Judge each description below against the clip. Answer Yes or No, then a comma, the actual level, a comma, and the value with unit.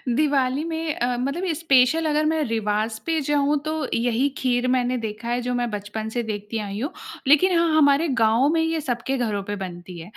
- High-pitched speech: Yes, very high, 250 Hz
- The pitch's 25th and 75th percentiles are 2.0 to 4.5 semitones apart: No, average, 5.3 semitones